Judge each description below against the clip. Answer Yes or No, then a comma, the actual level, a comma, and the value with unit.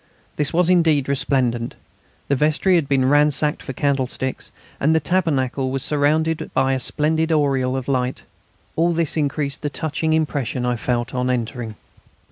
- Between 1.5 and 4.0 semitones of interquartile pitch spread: Yes, average, 3.4 semitones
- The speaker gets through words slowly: No, average, 155 wpm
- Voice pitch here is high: No, medium, 140 Hz